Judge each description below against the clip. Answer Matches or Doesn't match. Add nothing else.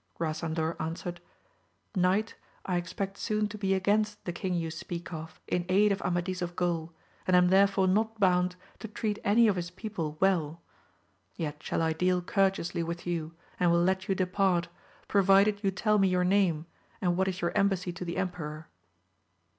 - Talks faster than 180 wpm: Matches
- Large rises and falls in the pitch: Doesn't match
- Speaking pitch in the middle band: Matches